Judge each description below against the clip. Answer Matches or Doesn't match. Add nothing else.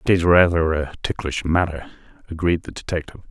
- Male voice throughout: Matches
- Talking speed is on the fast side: Doesn't match